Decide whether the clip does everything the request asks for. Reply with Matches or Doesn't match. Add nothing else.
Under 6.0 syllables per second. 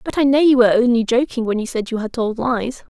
Doesn't match